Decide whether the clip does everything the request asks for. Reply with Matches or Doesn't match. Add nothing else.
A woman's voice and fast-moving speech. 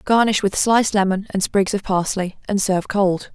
Doesn't match